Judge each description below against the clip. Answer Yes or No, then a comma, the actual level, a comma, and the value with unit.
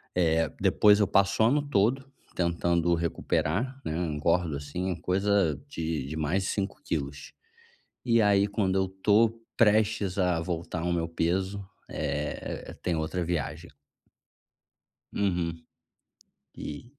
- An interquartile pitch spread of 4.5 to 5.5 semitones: No, average, 3.7 semitones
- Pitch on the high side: No, very low, 90 Hz